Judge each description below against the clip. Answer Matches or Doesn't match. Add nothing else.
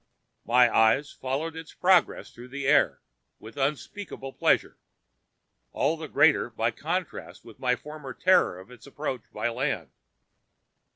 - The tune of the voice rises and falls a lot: Doesn't match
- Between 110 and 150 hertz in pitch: Matches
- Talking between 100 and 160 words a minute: Matches